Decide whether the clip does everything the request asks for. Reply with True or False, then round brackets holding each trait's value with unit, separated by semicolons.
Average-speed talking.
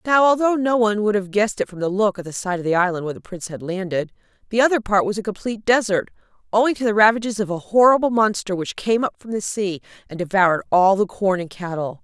False (250 wpm)